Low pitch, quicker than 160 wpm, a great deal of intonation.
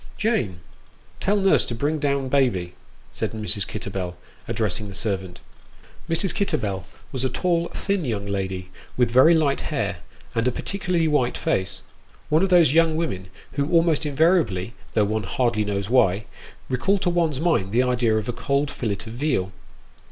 Yes: low, 125 Hz; average, 170 wpm; wide, 7.9 semitones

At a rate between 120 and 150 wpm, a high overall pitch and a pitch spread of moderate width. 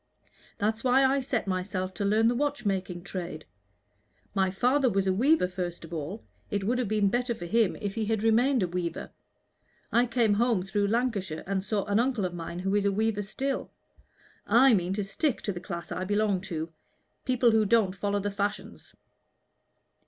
No: average, 190 wpm; high, 205 Hz; average, 3.8 semitones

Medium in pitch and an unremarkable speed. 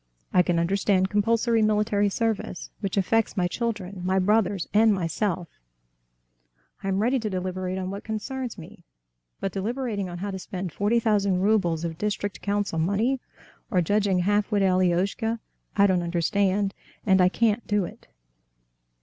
No: high, 200 Hz; average, 155 wpm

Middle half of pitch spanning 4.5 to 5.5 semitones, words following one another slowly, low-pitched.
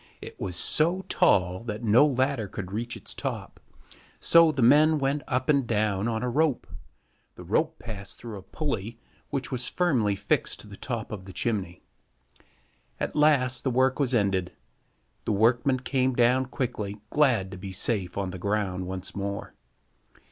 No: average, 4.9 semitones; average, 170 wpm; low, 115 Hz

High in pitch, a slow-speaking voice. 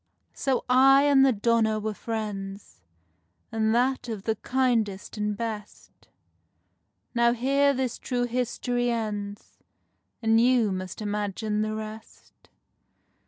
Yes: high, 225 Hz; slow, 120 wpm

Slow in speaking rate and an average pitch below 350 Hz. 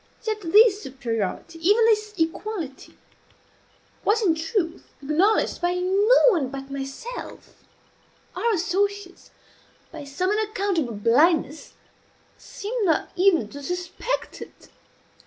No: slow, 105 wpm; very high, 360 Hz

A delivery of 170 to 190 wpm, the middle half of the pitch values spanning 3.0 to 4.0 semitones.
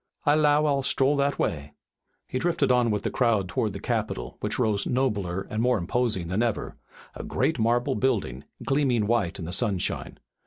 No: average, 185 wpm; average, 5.2 semitones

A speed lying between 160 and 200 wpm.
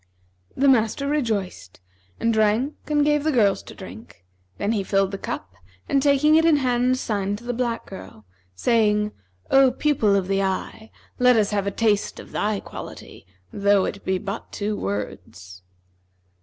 Yes: average, 170 wpm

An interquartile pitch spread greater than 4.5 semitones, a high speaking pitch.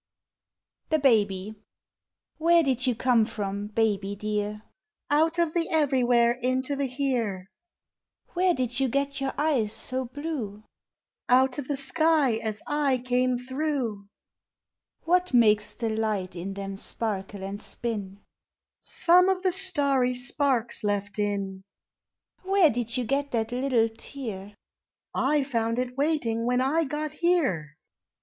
Yes: average, 5.1 semitones; very high, 250 Hz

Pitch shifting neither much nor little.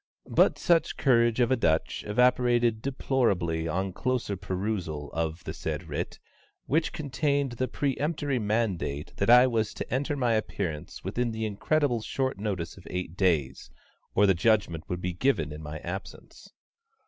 No: wide, 6.5 semitones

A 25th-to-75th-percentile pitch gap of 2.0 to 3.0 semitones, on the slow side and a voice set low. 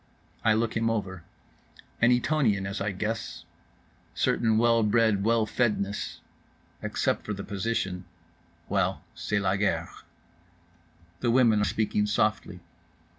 Yes: narrow, 2.6 semitones; slow, 120 wpm; low, 105 Hz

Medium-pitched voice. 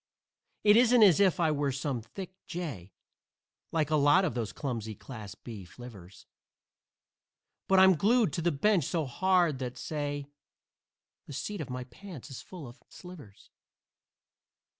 Yes: medium, 145 Hz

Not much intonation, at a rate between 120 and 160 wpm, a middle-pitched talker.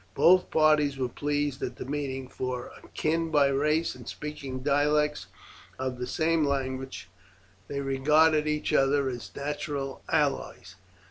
Yes: narrow, 2.2 semitones; slow, 135 wpm; medium, 145 Hz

